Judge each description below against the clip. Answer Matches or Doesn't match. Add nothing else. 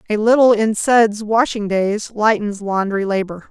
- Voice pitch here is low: Doesn't match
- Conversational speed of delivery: Matches